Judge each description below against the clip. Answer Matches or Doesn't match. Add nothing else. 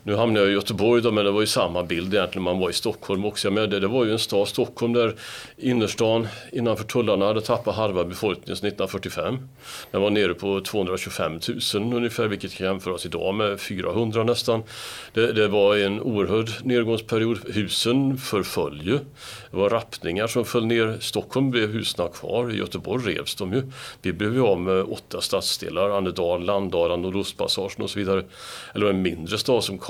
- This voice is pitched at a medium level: Doesn't match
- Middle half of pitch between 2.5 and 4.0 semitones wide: Matches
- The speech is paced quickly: Doesn't match